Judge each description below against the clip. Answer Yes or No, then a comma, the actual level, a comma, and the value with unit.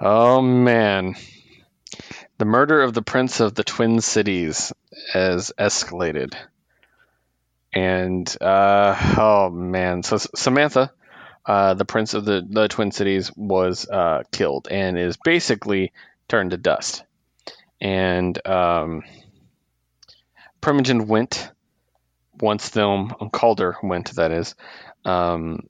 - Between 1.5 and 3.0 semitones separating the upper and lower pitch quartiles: No, average, 3.5 semitones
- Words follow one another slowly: Yes, slow, 110 wpm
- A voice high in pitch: No, low, 100 Hz